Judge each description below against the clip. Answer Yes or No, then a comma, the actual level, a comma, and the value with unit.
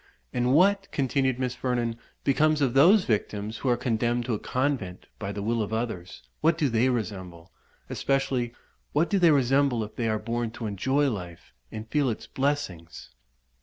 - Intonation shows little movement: No, average, 4.2 semitones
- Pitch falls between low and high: No, low, 120 Hz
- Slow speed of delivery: No, average, 175 wpm